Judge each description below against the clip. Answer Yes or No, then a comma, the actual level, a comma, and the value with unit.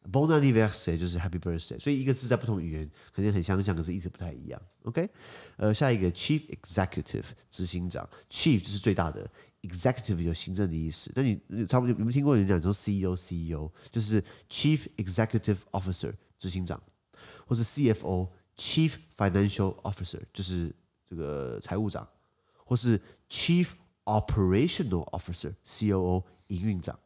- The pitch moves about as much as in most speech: Yes, average, 4.0 semitones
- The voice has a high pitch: No, low, 100 Hz